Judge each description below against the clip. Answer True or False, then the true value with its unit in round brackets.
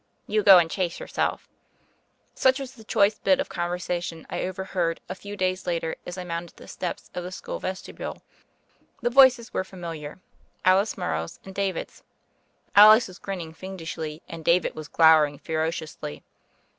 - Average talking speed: True (160 wpm)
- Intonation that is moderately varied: True (3.3 semitones)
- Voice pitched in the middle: True (180 Hz)